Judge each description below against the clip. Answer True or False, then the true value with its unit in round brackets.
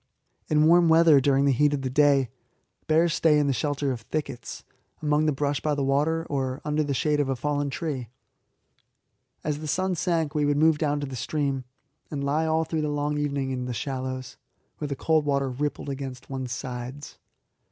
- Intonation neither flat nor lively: False (2.3 semitones)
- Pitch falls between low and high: True (145 Hz)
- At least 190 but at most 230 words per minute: True (200 wpm)